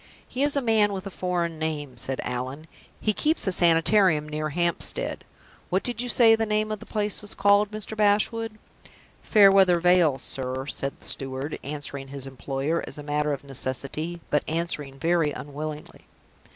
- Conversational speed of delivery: Yes, average, 160 wpm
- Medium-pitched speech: Yes, medium, 165 Hz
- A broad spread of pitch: Yes, wide, 6.4 semitones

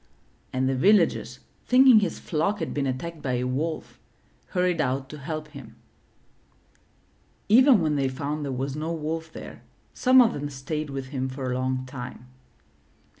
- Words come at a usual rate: Yes, average, 170 wpm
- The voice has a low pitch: No, medium, 145 Hz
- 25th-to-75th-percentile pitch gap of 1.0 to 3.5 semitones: No, average, 4.1 semitones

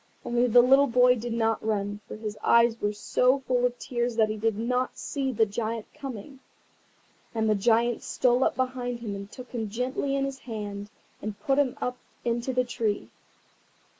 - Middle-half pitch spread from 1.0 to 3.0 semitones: Yes, narrow, 2.6 semitones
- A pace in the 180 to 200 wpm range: Yes, average, 190 wpm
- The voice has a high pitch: Yes, high, 240 Hz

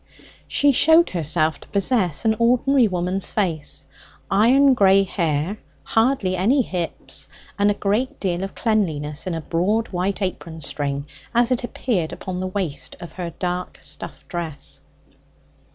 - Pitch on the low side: No, high, 190 Hz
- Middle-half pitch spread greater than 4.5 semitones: Yes, average, 4.9 semitones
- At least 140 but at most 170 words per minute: Yes, average, 145 wpm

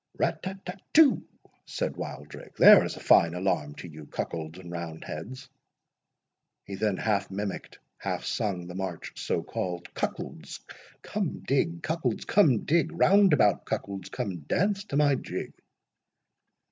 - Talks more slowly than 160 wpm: Yes, average, 145 wpm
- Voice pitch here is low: Yes, low, 100 Hz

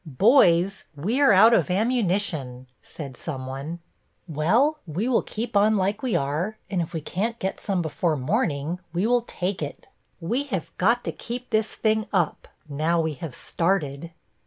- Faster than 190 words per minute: No, average, 165 wpm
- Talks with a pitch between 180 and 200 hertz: Yes, medium, 185 Hz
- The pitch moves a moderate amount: No, wide, 5.8 semitones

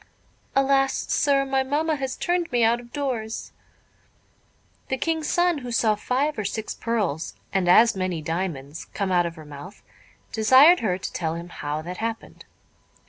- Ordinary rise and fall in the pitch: No, wide, 7.1 semitones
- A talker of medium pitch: No, high, 225 Hz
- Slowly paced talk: No, average, 165 wpm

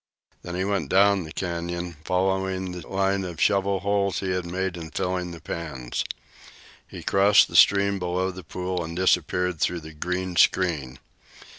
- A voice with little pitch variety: Yes, narrow, 1.9 semitones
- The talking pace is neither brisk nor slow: Yes, average, 165 wpm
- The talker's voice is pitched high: No, very low, 90 Hz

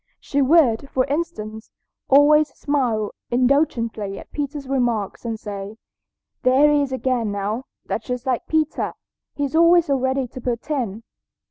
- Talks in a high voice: Yes, very high, 260 Hz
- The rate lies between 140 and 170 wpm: Yes, average, 145 wpm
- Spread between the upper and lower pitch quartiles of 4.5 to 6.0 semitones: No, average, 4.1 semitones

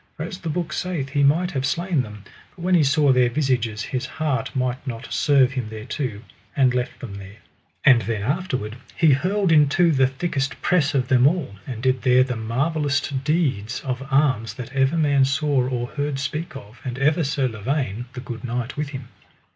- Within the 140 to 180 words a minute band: No, average, 195 wpm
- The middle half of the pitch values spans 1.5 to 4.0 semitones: Yes, average, 3.4 semitones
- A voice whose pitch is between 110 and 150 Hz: Yes, low, 135 Hz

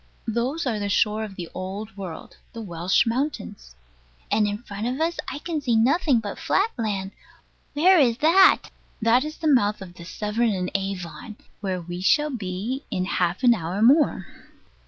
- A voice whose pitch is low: No, high, 215 Hz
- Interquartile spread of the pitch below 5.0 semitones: No, wide, 5.4 semitones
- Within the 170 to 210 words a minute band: Yes, average, 180 wpm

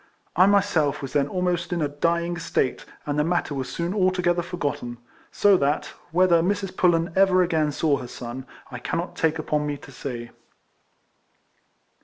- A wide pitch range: No, average, 3.8 semitones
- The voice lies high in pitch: No, medium, 165 Hz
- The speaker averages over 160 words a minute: Yes, average, 170 wpm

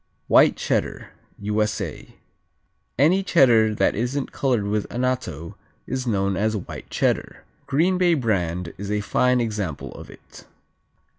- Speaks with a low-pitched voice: Yes, low, 110 Hz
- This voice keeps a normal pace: No, slow, 130 wpm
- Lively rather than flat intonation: No, average, 4.4 semitones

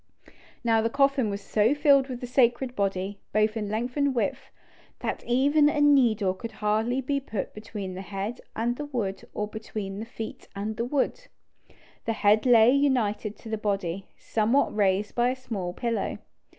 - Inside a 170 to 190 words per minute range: Yes, average, 175 wpm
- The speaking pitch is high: Yes, high, 225 Hz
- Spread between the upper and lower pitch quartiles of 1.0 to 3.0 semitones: No, average, 3.8 semitones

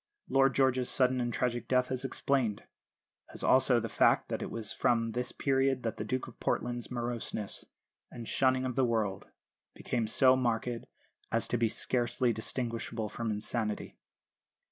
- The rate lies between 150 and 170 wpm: Yes, average, 160 wpm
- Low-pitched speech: Yes, low, 120 Hz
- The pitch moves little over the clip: Yes, narrow, 2.0 semitones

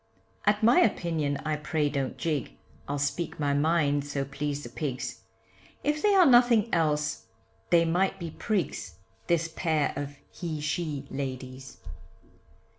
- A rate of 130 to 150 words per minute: Yes, average, 140 wpm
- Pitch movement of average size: Yes, average, 3.4 semitones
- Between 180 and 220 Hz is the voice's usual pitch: No, medium, 150 Hz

